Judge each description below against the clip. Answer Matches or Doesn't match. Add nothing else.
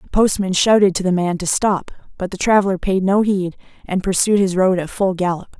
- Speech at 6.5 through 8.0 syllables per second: Doesn't match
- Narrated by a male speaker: Doesn't match